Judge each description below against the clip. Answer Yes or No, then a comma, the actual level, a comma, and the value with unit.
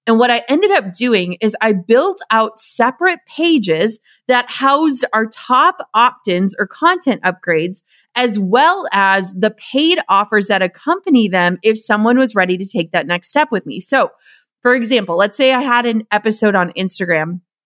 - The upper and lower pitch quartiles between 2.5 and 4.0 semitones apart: No, average, 4.9 semitones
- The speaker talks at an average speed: Yes, average, 175 wpm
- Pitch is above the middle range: Yes, high, 220 Hz